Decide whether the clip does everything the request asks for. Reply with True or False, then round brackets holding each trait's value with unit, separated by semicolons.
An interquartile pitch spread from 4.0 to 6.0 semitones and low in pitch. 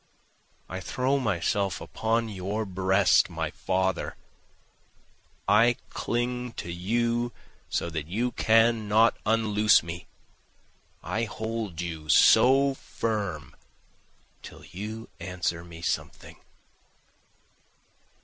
True (4.4 semitones; 105 Hz)